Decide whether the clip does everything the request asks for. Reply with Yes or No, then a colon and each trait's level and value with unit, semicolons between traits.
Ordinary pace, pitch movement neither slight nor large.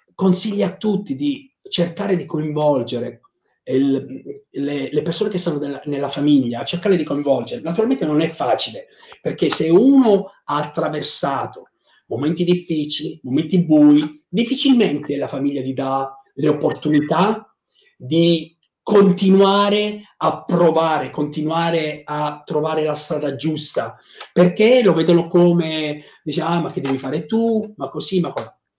Yes: average, 135 wpm; average, 4.8 semitones